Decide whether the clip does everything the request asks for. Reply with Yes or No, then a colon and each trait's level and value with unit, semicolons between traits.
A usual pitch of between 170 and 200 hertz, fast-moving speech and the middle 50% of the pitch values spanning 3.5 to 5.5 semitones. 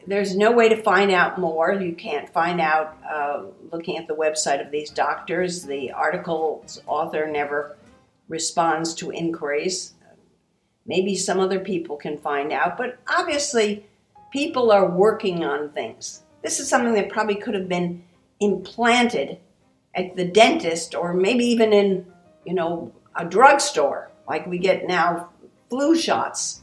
No: medium, 185 Hz; average, 150 wpm; average, 4.1 semitones